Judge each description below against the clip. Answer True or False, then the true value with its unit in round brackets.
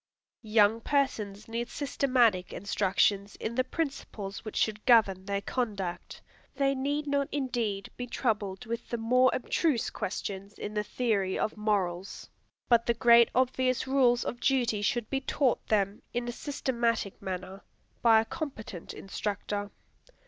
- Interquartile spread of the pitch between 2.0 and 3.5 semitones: False (4.0 semitones)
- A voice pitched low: False (225 Hz)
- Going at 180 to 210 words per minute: False (140 wpm)